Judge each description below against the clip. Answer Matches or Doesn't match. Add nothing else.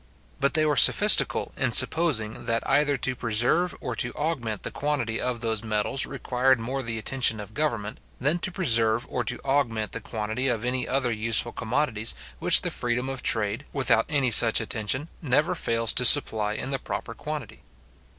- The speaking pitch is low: Matches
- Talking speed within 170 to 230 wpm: Matches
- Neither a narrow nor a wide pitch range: Matches